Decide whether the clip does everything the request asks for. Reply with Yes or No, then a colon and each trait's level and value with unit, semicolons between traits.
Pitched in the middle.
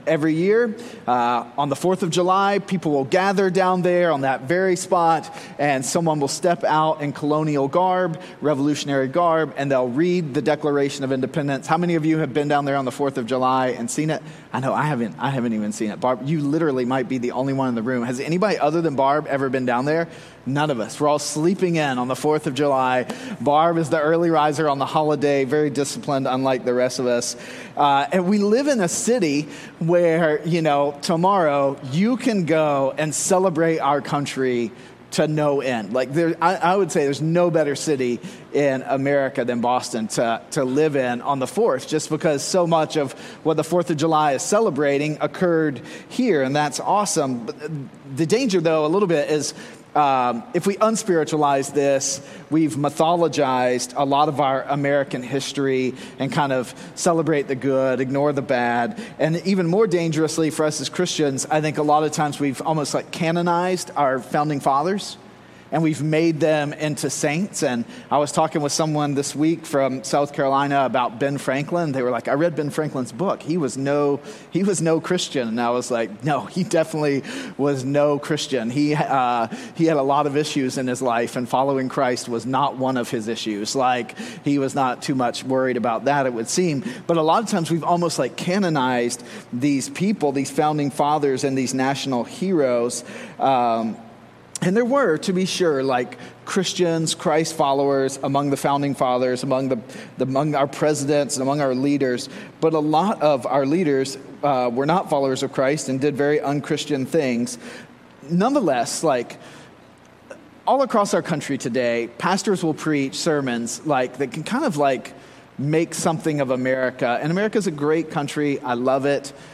Yes: medium, 145 Hz